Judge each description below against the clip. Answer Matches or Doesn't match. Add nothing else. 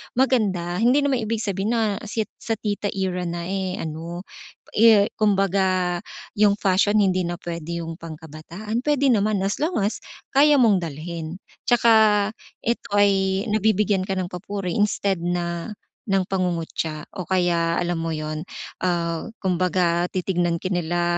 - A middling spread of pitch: Matches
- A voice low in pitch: Doesn't match